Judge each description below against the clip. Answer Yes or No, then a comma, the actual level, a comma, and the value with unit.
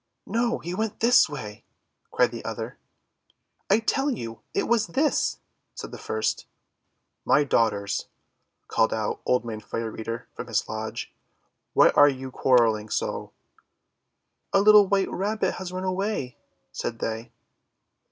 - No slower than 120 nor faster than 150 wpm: Yes, average, 140 wpm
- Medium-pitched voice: Yes, medium, 145 Hz